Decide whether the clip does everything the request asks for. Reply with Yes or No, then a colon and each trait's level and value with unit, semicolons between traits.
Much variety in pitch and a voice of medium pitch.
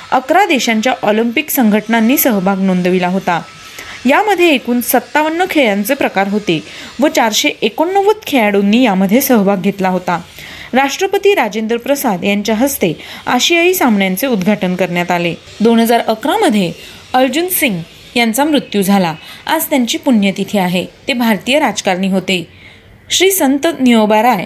No: wide, 6.2 semitones; high, 235 Hz